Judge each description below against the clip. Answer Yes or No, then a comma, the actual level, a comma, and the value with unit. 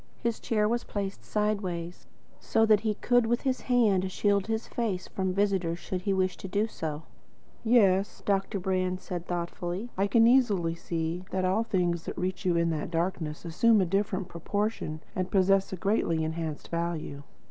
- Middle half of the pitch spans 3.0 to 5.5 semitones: Yes, average, 3.4 semitones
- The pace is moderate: Yes, average, 180 wpm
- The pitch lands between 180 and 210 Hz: Yes, high, 190 Hz